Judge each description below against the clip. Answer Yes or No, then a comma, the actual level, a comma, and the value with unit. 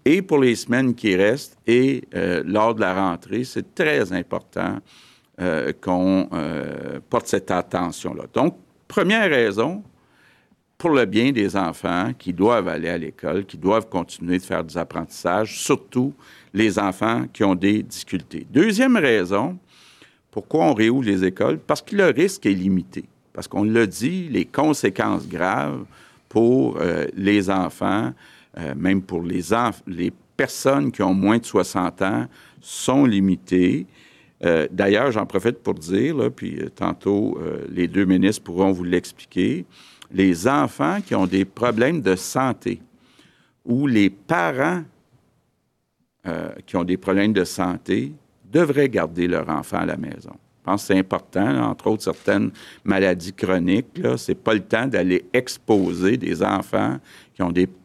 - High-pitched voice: No, very low, 95 Hz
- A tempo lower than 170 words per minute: Yes, average, 160 wpm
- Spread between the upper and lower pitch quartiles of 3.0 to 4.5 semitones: Yes, average, 4.2 semitones